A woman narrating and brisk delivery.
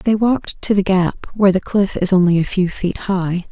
Yes: female; fast, 240 wpm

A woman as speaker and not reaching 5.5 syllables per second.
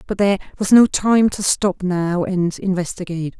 Yes: female; 5.0 syllables/s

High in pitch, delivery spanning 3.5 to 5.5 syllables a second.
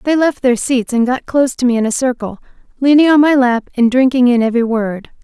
No: very high, 250 Hz; 5.9 syllables/s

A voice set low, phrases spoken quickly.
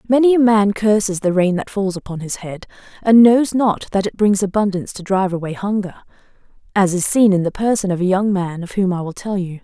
No: high, 195 Hz; fast, 235 wpm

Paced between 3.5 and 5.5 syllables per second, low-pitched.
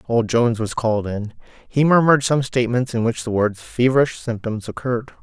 No: 5.7 syllables/s; low, 120 Hz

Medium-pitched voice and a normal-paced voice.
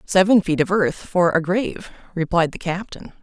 Yes: medium, 180 Hz; average, 185 wpm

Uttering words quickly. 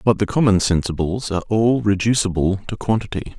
No: average, 160 wpm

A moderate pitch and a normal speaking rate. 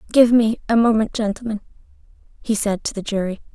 No: high, 215 Hz; average, 170 wpm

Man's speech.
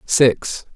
Yes: male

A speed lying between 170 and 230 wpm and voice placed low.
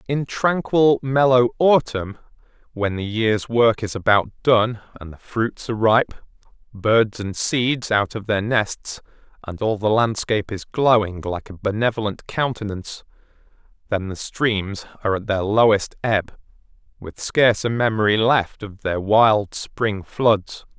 No: average, 145 wpm; low, 110 Hz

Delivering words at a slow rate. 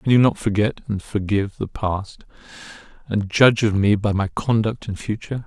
No: average, 185 wpm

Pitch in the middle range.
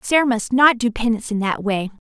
No: high, 230 Hz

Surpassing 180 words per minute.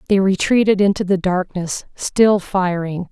No: slow, 135 wpm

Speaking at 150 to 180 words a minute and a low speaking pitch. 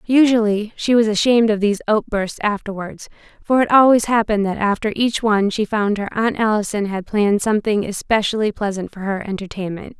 No: average, 175 wpm; high, 210 Hz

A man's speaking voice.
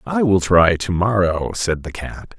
Yes: male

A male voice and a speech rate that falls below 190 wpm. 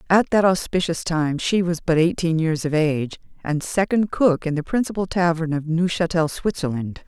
No: female; average, 180 wpm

